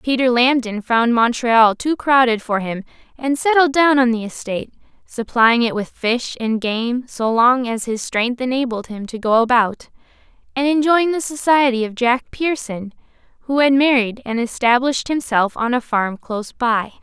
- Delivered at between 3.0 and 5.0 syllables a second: Yes, 4.6 syllables/s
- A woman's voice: Yes, female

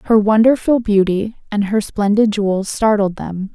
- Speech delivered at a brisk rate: No, average, 150 wpm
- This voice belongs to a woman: Yes, female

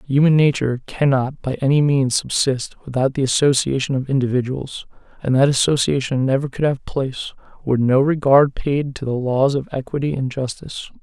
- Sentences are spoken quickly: No, average, 165 wpm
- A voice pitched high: No, low, 135 Hz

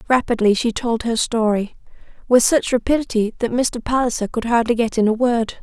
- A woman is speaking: Yes, female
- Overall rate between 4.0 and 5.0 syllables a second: No, 5.3 syllables/s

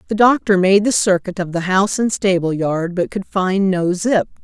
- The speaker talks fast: Yes, fast, 215 wpm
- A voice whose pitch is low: No, high, 190 Hz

